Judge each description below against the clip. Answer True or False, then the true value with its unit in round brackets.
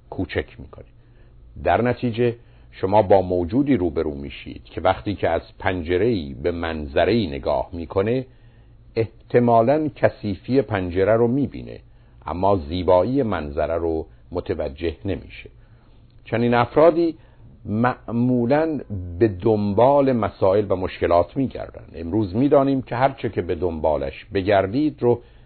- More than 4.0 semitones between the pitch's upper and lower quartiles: True (5.1 semitones)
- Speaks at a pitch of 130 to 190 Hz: False (115 Hz)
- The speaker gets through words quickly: False (110 wpm)